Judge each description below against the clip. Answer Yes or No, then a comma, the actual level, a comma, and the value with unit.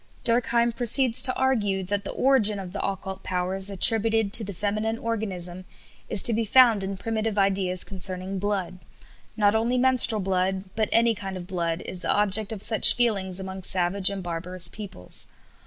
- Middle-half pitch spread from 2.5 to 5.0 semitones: Yes, average, 3.1 semitones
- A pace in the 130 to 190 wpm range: Yes, average, 170 wpm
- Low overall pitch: No, high, 200 Hz